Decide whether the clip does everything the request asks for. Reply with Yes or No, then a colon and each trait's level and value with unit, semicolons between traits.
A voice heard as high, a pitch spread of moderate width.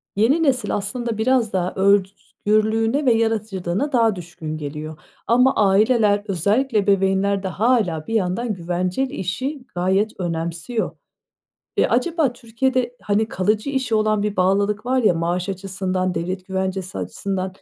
Yes: high, 205 Hz; average, 3.9 semitones